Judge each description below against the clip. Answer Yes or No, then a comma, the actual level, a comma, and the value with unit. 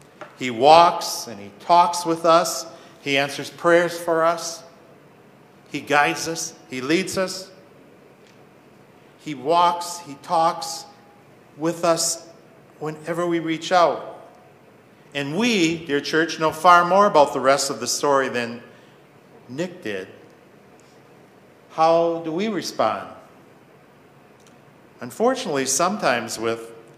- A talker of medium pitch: Yes, medium, 165 Hz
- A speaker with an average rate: No, slow, 115 wpm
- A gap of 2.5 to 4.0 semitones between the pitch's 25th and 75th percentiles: Yes, average, 3.2 semitones